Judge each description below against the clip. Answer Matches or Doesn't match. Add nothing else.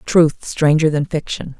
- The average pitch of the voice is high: Doesn't match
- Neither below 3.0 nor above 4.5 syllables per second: Matches